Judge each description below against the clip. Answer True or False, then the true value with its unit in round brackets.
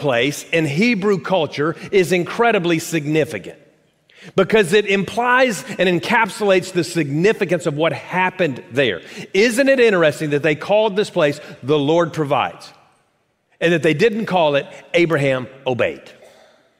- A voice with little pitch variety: False (5.0 semitones)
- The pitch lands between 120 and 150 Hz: False (175 Hz)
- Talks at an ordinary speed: False (130 wpm)